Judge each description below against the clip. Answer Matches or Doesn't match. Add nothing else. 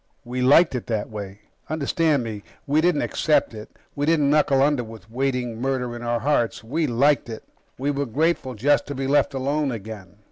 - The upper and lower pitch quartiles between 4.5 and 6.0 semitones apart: Doesn't match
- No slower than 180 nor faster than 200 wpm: Matches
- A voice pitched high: Doesn't match